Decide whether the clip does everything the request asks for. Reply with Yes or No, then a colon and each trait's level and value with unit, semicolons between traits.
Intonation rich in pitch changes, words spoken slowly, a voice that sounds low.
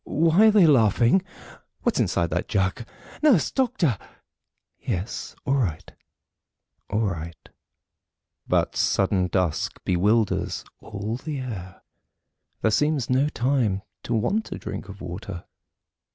Yes: wide, 7.2 semitones; slow, 120 wpm; low, 110 Hz